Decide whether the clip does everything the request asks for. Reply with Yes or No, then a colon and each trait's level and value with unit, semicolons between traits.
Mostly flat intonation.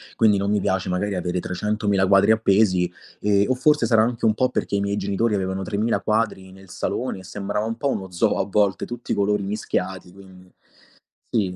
Yes: narrow, 2.3 semitones